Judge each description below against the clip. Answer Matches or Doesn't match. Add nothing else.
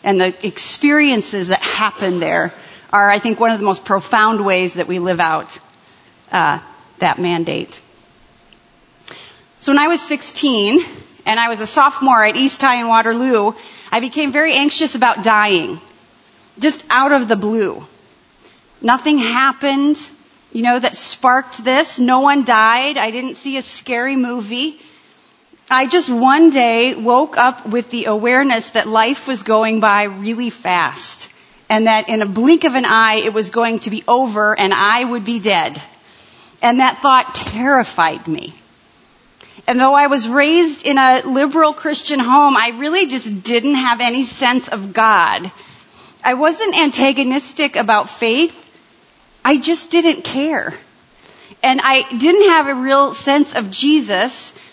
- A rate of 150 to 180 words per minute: Matches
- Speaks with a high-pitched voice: Matches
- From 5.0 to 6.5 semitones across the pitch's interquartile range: Doesn't match